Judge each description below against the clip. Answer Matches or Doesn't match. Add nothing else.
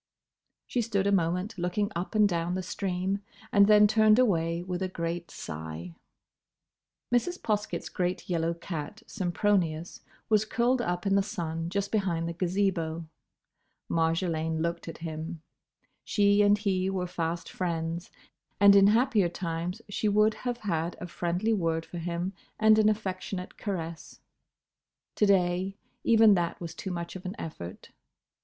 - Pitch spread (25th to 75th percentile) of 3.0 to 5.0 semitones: Matches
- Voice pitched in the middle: Matches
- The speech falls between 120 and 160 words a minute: Matches